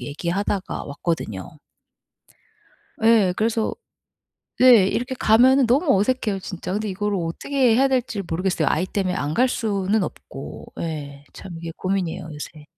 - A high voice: Yes, high, 195 Hz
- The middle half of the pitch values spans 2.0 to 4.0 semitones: No, wide, 5.5 semitones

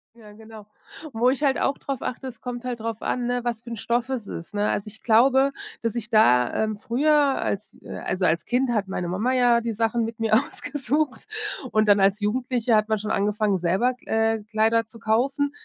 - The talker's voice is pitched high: Yes, high, 225 Hz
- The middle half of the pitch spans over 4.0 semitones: No, narrow, 2.6 semitones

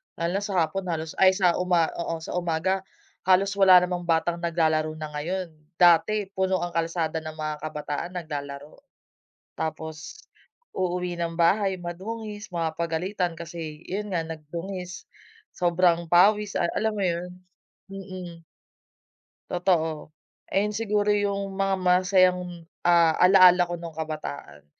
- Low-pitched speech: No, medium, 175 Hz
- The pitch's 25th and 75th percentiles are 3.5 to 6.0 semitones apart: No, average, 2.7 semitones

